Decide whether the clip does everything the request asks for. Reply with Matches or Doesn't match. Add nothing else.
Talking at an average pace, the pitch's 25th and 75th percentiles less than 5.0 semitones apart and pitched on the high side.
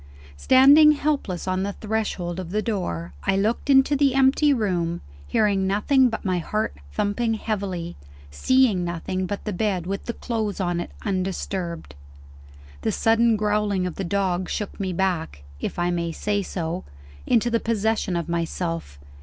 Matches